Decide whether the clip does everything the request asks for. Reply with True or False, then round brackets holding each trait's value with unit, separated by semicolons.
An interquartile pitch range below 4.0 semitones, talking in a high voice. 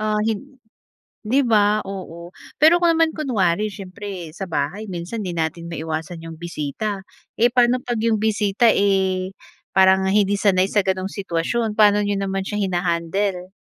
True (3.3 semitones; 195 Hz)